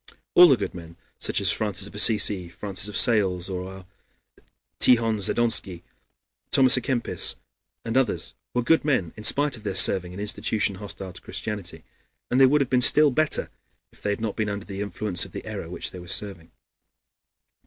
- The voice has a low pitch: Yes, low, 105 Hz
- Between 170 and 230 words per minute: Yes, average, 190 wpm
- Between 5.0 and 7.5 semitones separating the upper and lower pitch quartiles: No, average, 4.3 semitones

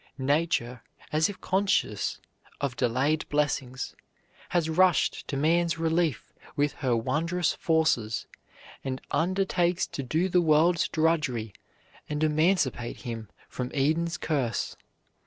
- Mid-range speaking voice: Yes, medium, 155 Hz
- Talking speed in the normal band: No, slow, 115 wpm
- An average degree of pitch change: Yes, average, 4.5 semitones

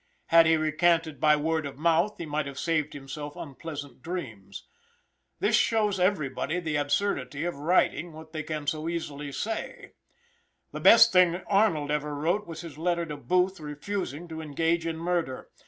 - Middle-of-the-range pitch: Yes, medium, 160 Hz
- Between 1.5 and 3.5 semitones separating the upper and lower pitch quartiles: Yes, average, 2.8 semitones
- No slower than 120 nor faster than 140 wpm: No, average, 165 wpm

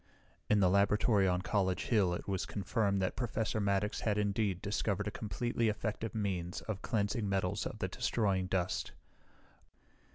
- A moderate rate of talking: Yes, average, 155 wpm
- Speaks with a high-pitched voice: No, low, 100 Hz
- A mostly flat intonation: Yes, narrow, 2.2 semitones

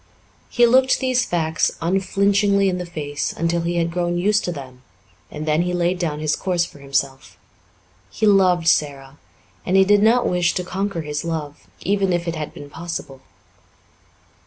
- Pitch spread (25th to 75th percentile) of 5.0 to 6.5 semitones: No, average, 4.1 semitones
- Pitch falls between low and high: Yes, medium, 175 Hz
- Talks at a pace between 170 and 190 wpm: Yes, average, 175 wpm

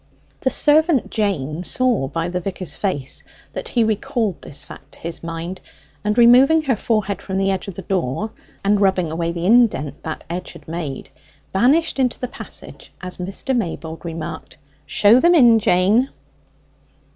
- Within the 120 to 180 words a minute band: Yes, average, 165 wpm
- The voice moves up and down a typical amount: No, wide, 6.0 semitones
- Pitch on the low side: No, high, 195 Hz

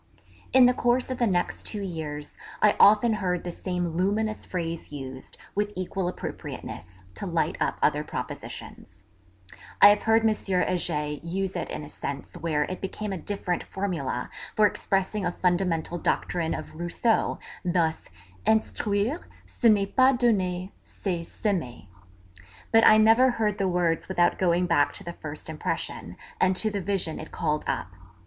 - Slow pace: No, average, 160 wpm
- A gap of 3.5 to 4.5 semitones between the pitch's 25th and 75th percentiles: Yes, average, 3.9 semitones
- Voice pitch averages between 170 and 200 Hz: Yes, medium, 185 Hz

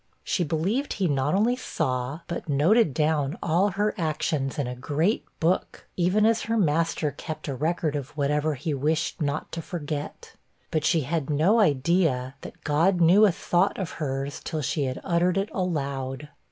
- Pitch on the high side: No, medium, 155 Hz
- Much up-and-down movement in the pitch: No, average, 4.1 semitones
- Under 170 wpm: No, average, 175 wpm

